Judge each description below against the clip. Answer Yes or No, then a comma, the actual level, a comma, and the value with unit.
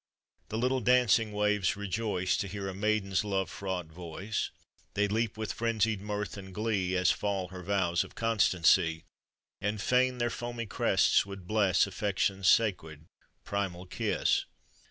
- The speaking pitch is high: No, low, 100 Hz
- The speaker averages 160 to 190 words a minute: No, average, 145 wpm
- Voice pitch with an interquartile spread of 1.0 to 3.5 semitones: Yes, average, 2.8 semitones